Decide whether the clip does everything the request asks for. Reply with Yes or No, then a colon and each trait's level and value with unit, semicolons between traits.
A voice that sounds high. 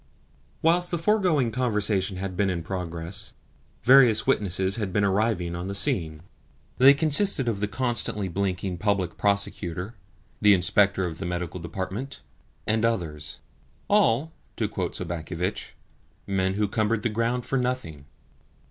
No: low, 100 Hz